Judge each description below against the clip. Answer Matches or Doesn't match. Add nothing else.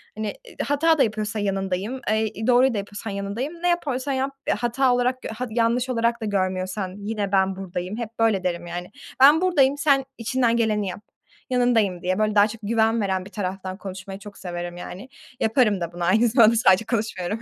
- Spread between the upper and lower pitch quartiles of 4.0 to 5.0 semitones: Matches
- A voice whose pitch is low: Doesn't match